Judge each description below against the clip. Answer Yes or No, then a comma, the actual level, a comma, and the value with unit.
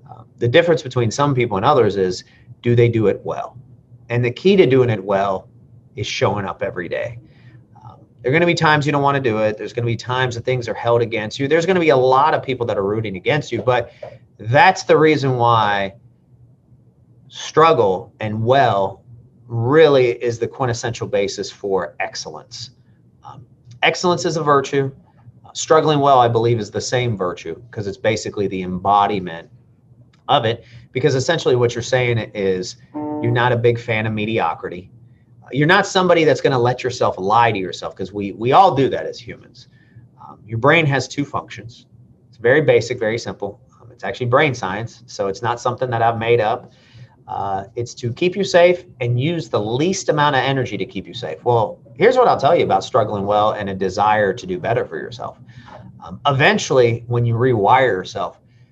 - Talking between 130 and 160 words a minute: No, average, 195 wpm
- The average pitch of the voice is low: Yes, low, 120 Hz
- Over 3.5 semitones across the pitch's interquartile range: No, average, 2.9 semitones